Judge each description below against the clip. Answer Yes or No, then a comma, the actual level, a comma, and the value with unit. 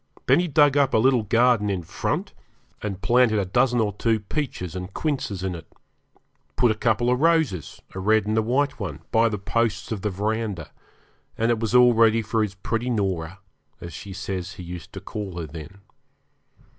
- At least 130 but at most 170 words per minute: No, average, 195 wpm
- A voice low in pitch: Yes, low, 110 Hz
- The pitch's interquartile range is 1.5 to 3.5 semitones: No, average, 4.0 semitones